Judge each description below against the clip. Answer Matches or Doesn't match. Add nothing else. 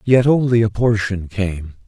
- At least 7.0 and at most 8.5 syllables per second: Doesn't match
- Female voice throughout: Doesn't match